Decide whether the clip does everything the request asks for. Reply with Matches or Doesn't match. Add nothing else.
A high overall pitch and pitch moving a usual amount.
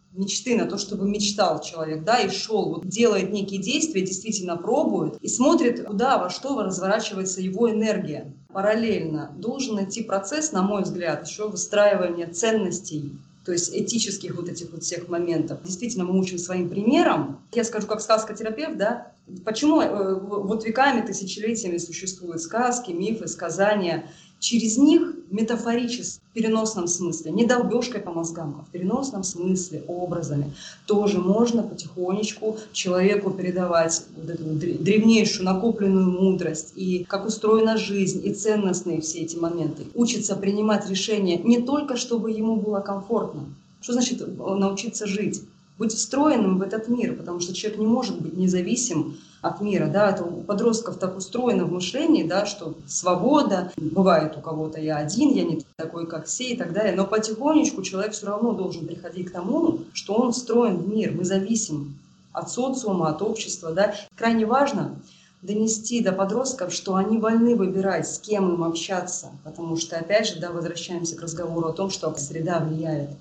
Matches